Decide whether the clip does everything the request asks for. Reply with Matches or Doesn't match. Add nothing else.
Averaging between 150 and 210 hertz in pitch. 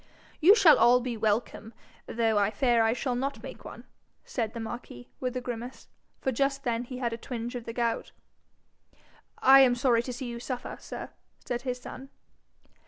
Doesn't match